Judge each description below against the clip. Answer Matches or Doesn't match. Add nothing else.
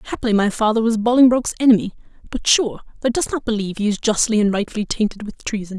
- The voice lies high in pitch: Matches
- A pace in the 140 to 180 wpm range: Doesn't match